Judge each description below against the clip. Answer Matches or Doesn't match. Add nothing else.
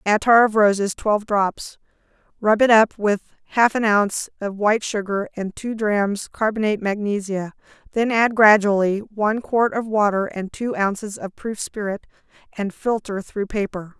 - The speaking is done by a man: Doesn't match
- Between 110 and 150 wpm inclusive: Doesn't match